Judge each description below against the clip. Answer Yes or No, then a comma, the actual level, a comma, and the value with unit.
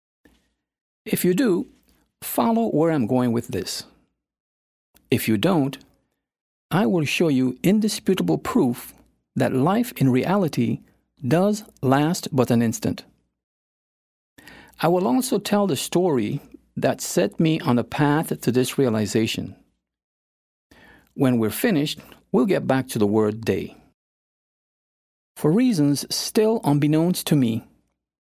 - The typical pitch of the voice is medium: No, low, 130 Hz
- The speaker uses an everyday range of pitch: No, wide, 8.1 semitones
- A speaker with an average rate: No, slow, 125 wpm